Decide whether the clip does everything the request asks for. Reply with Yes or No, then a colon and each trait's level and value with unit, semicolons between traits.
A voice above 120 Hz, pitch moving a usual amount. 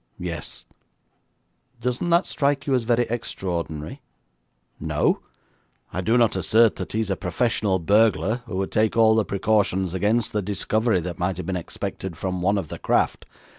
No: low, 105 Hz; average, 3.9 semitones